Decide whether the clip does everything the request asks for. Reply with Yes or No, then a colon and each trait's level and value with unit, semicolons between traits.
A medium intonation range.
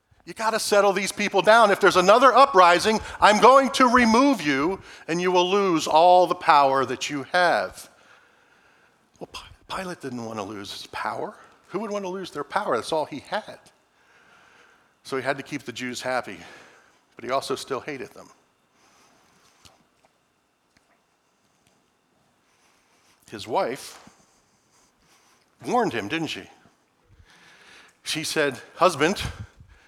No: wide, 7.0 semitones